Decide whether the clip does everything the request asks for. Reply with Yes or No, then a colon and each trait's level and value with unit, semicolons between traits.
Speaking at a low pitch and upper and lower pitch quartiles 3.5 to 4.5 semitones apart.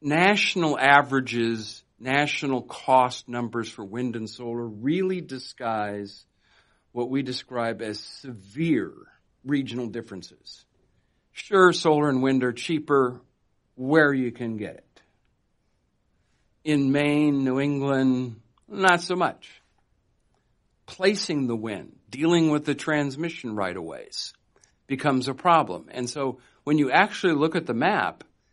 Yes: low, 130 Hz; average, 4.0 semitones